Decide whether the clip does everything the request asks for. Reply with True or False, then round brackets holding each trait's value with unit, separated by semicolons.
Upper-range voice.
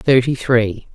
False (120 Hz)